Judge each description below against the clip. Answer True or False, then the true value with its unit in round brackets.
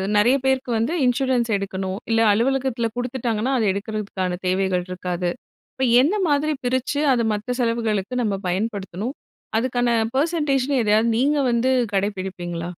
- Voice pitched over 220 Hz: True (230 Hz)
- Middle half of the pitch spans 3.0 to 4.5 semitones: False (4.9 semitones)